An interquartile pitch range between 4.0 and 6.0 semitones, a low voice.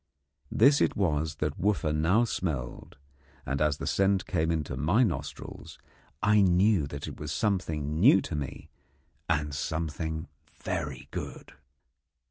Yes: average, 4.3 semitones; very low, 80 Hz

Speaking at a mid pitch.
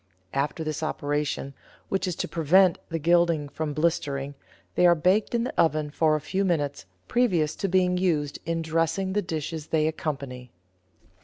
Yes: medium, 160 Hz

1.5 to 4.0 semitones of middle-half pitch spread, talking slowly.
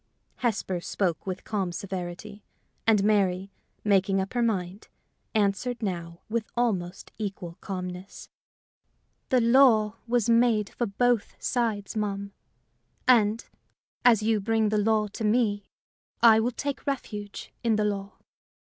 Yes: average, 2.8 semitones; slow, 130 wpm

